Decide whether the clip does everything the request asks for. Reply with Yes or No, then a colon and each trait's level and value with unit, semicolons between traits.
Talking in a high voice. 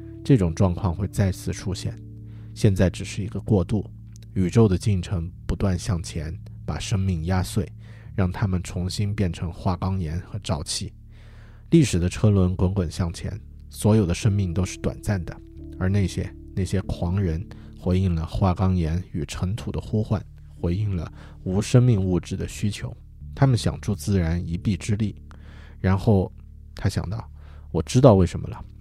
No: very low, 95 Hz